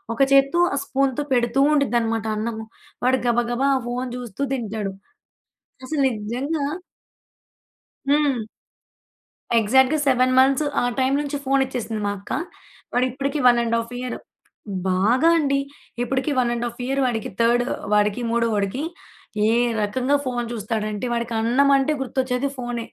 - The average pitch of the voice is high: Yes, very high, 250 Hz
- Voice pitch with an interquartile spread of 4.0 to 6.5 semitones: No, average, 2.8 semitones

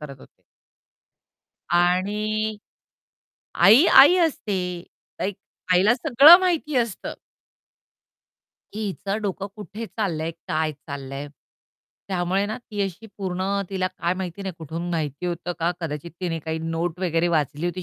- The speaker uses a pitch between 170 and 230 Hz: Yes, medium, 185 Hz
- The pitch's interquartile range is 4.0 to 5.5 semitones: Yes, average, 4.3 semitones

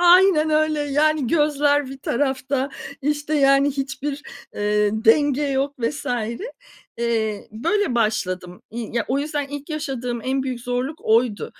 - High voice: Yes, very high, 275 Hz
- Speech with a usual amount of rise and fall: Yes, average, 3.9 semitones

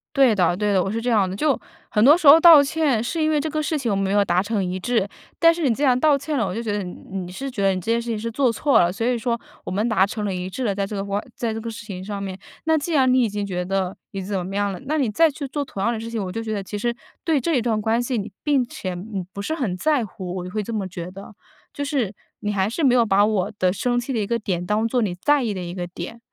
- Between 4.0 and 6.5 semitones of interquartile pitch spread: Yes, average, 4.8 semitones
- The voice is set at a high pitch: Yes, high, 220 Hz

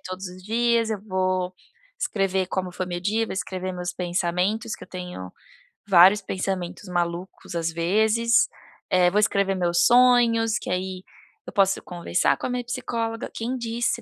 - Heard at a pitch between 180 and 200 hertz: Yes, high, 190 Hz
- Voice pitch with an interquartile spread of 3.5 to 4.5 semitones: Yes, average, 3.9 semitones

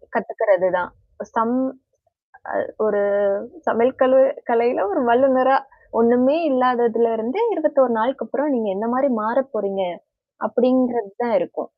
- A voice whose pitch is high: Yes, high, 240 Hz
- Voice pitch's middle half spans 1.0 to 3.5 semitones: Yes, average, 2.7 semitones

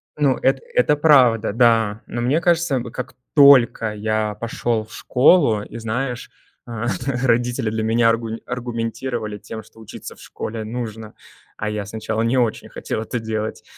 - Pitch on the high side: No, low, 115 Hz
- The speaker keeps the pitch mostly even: Yes, narrow, 2.3 semitones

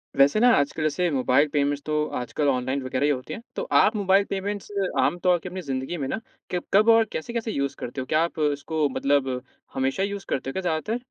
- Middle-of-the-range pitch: Yes, medium, 155 Hz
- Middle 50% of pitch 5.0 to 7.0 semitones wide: Yes, wide, 5.6 semitones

